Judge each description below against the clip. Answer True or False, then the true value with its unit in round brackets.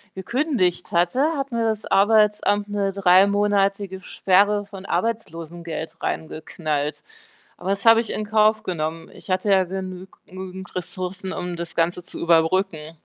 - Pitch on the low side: False (190 Hz)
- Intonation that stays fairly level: False (3.0 semitones)